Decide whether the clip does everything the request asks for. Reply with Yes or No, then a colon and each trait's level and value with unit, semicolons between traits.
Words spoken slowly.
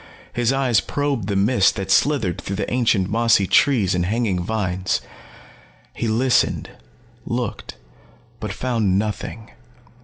Yes: slow, 125 wpm